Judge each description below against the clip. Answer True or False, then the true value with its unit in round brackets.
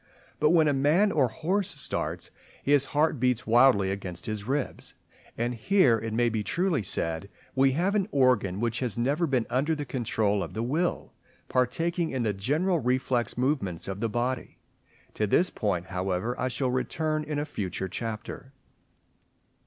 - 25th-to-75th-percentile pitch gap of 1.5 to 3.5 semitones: False (5.5 semitones)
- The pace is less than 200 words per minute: True (170 wpm)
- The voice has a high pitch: False (125 Hz)